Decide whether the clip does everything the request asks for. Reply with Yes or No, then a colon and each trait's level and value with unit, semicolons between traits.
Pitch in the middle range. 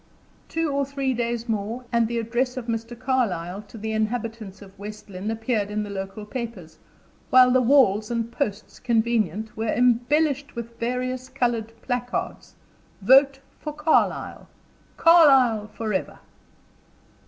No: high, 235 Hz